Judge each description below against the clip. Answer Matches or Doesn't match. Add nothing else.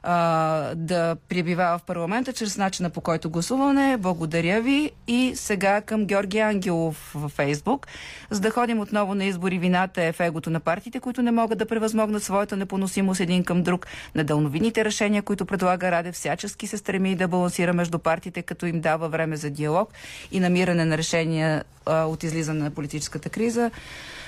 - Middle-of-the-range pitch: Matches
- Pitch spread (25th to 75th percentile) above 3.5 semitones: Matches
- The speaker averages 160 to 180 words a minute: Matches